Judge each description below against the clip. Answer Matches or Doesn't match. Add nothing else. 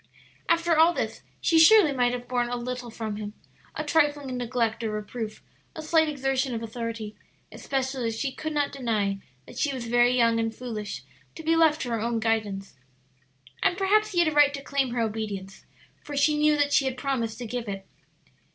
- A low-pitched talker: Doesn't match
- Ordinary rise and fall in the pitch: Matches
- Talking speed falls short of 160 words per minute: Doesn't match